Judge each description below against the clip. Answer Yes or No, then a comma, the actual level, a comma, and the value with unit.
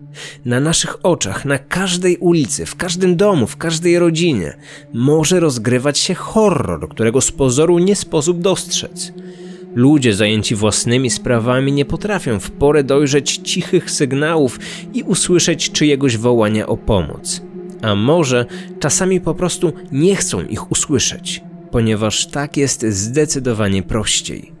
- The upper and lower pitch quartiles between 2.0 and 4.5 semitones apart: No, wide, 5.6 semitones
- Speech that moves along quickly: No, average, 130 wpm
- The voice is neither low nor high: Yes, medium, 155 Hz